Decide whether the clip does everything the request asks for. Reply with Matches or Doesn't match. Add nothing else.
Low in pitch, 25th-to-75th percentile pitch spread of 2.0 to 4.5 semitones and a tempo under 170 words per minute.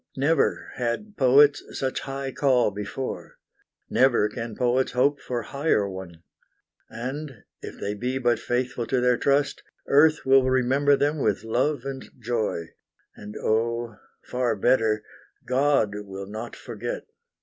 Matches